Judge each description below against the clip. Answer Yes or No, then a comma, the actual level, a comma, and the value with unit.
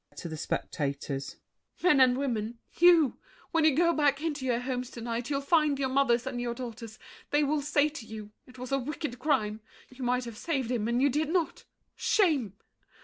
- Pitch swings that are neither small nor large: Yes, average, 3.9 semitones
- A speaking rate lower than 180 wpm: No, average, 195 wpm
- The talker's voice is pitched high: Yes, very high, 260 Hz